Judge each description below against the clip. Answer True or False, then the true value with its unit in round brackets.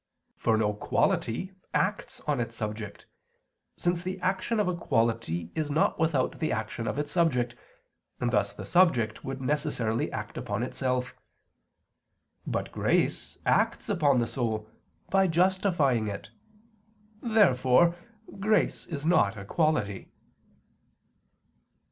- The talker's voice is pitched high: False (135 Hz)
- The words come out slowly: True (125 wpm)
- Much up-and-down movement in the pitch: True (7.2 semitones)